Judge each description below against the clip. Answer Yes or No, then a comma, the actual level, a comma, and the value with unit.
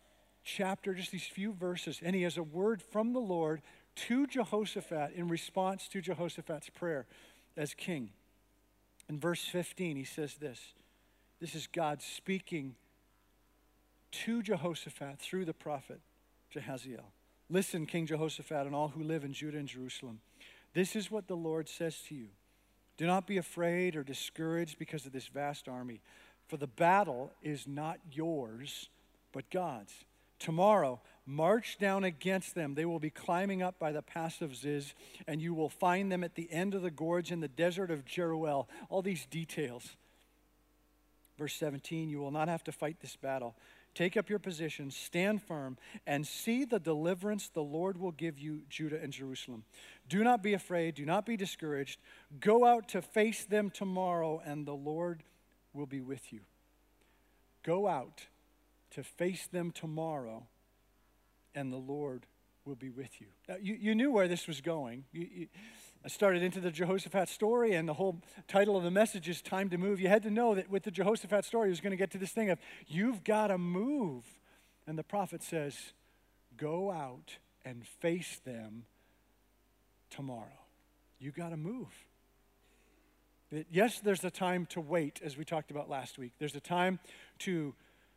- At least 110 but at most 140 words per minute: No, average, 170 wpm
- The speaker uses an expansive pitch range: No, average, 4.8 semitones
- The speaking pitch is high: No, medium, 165 Hz